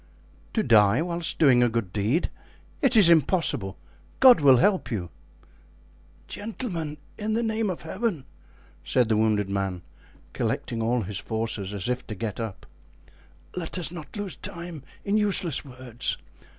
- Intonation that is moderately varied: No, wide, 8.6 semitones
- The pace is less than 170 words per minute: Yes, average, 150 wpm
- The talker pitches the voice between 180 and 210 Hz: No, low, 135 Hz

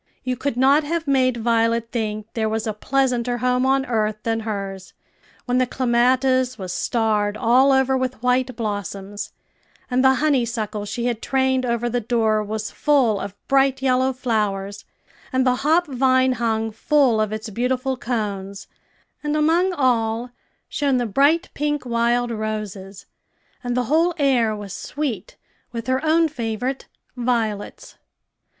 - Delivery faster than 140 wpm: Yes, average, 150 wpm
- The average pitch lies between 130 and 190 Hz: No, high, 245 Hz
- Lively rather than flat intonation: No, average, 3.2 semitones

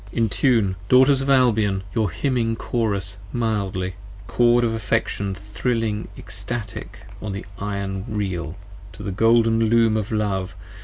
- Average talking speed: No, slow, 125 wpm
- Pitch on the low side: Yes, low, 110 Hz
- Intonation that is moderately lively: Yes, average, 3.0 semitones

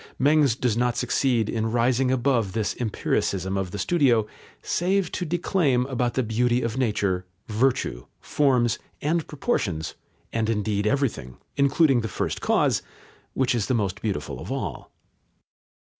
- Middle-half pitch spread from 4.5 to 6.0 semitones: No, average, 4.1 semitones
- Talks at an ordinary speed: Yes, average, 145 wpm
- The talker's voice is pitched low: Yes, low, 120 Hz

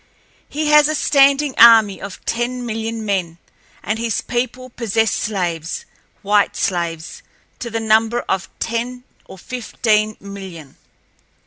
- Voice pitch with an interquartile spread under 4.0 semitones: Yes, average, 3.6 semitones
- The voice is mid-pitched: No, high, 225 Hz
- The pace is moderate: No, slow, 115 wpm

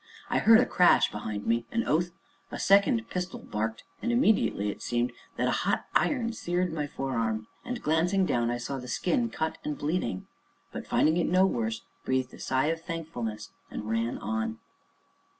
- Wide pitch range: Yes, wide, 8.0 semitones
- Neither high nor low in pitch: Yes, medium, 150 Hz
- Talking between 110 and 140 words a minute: No, average, 180 wpm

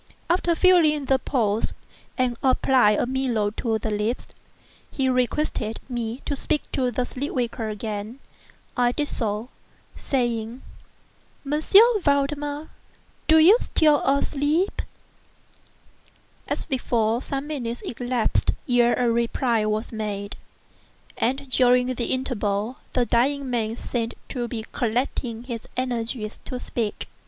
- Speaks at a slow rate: Yes, slow, 125 wpm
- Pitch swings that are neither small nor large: Yes, average, 3.2 semitones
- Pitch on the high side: Yes, high, 245 Hz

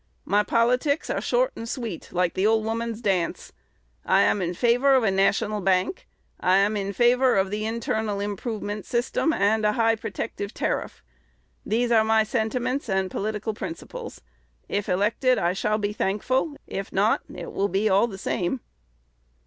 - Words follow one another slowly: No, average, 165 wpm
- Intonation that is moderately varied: Yes, average, 3.1 semitones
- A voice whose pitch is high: Yes, high, 215 Hz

